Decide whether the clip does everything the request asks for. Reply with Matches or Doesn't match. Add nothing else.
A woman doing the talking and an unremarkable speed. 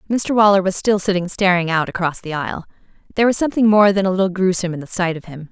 Doesn't match